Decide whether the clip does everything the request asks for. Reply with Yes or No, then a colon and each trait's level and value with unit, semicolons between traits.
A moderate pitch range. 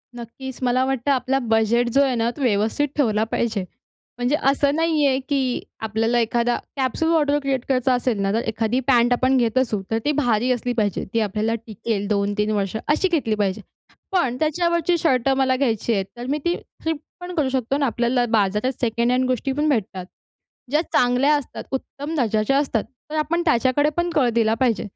Yes: average, 3.9 semitones